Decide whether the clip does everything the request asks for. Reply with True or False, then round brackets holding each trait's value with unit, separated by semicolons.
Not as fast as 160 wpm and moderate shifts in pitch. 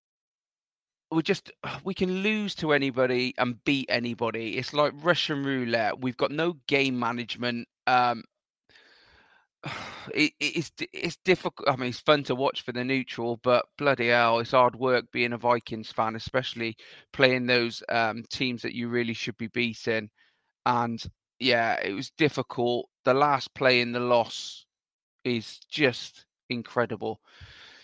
True (145 wpm; 3.0 semitones)